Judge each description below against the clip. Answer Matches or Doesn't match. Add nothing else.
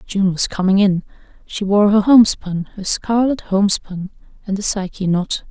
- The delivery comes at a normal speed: Matches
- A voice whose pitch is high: Matches